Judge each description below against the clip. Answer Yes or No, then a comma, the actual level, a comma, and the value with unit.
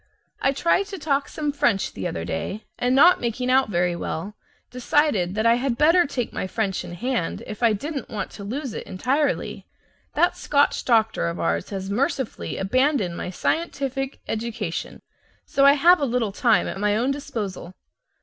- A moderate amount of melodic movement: No, wide, 6.0 semitones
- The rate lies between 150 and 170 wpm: No, average, 180 wpm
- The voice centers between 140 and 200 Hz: No, high, 240 Hz